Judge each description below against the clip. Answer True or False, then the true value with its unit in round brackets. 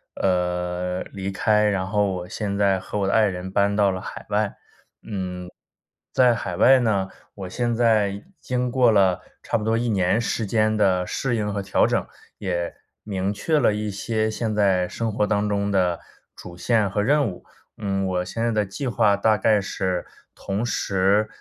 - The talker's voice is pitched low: True (100 Hz)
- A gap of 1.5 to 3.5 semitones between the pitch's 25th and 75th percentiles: True (2.6 semitones)